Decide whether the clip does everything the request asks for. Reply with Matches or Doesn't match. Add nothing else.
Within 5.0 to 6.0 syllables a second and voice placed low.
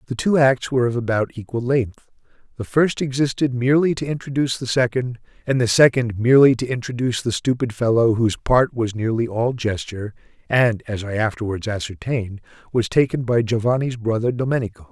Matches